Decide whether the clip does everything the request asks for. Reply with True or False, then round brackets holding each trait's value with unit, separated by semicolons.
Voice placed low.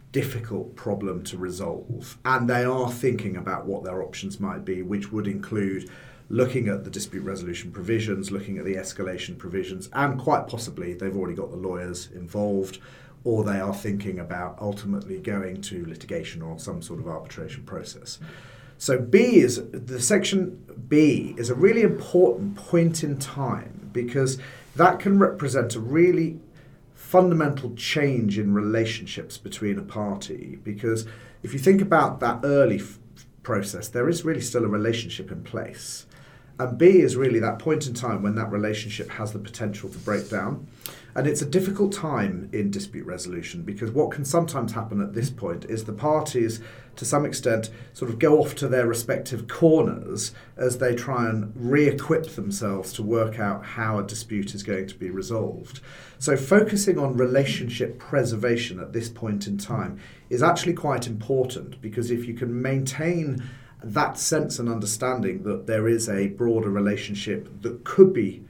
True (120 Hz)